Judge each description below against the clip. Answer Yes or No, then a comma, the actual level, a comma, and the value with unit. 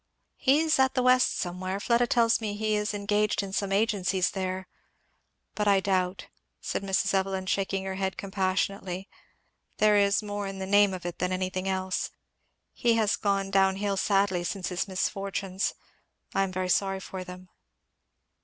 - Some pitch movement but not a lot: No, narrow, 1.7 semitones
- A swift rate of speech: No, average, 170 wpm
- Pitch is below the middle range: No, high, 195 Hz